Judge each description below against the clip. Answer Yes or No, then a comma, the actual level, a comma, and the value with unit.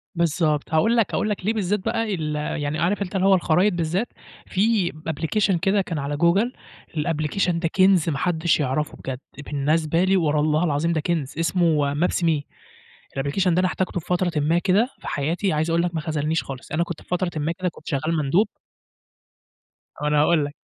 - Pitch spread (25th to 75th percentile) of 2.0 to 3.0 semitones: No, average, 3.5 semitones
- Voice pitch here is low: No, medium, 165 Hz